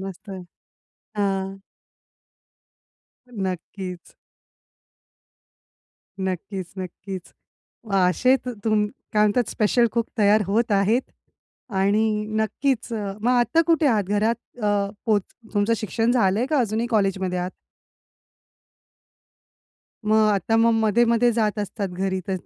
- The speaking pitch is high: Yes, high, 210 Hz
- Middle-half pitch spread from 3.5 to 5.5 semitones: No, average, 3.1 semitones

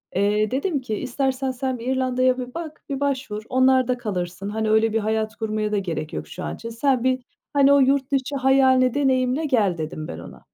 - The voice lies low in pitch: No, very high, 255 Hz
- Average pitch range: Yes, average, 3.6 semitones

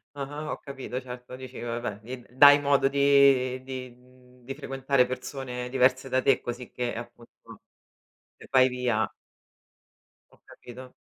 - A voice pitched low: Yes, low, 130 Hz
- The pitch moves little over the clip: Yes, narrow, 1.6 semitones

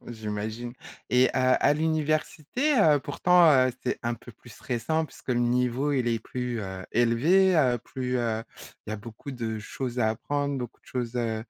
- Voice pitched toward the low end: Yes, low, 125 Hz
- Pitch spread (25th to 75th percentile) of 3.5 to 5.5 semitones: Yes, average, 3.8 semitones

